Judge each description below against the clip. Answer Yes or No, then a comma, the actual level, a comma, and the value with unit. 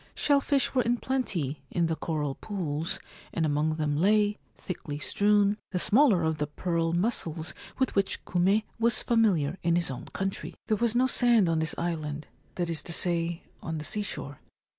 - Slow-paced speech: No, average, 185 wpm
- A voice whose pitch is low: No, medium, 175 Hz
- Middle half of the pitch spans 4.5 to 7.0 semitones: Yes, average, 5.0 semitones